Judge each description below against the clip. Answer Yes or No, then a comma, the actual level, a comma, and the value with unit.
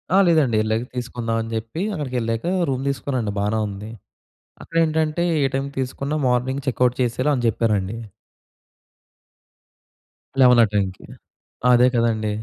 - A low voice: Yes, low, 125 Hz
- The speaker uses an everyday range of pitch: Yes, average, 3.4 semitones